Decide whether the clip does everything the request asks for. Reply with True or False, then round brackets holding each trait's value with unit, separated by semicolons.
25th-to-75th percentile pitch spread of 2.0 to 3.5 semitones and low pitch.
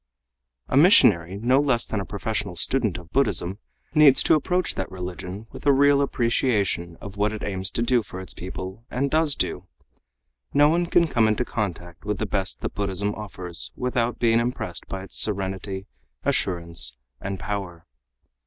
False (5.0 semitones; 105 Hz)